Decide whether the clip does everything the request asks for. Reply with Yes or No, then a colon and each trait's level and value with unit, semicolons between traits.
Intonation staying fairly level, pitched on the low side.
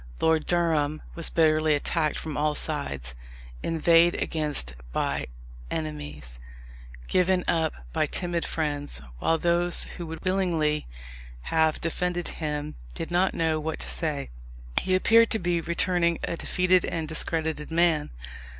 No: narrow, 2.3 semitones; medium, 160 Hz